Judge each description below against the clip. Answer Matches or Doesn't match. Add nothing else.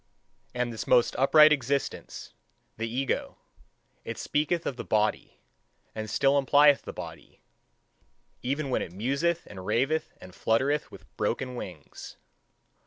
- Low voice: Matches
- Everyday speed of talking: Doesn't match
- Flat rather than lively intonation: Doesn't match